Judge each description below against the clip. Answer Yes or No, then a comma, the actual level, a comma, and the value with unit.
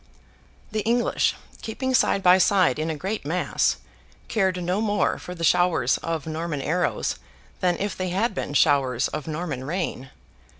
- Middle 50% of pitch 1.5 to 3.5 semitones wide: No, average, 4.1 semitones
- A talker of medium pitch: Yes, medium, 180 Hz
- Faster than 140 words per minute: Yes, average, 160 wpm